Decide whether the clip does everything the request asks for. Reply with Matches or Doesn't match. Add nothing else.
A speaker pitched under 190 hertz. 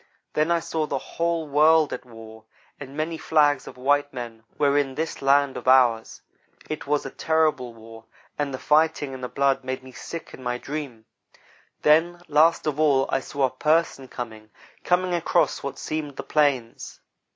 Matches